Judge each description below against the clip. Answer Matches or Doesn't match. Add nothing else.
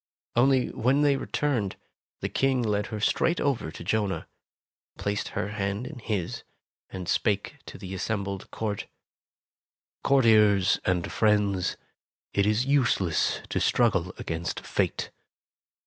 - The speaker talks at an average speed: Doesn't match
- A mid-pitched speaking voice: Doesn't match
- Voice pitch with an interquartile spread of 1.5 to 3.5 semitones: Doesn't match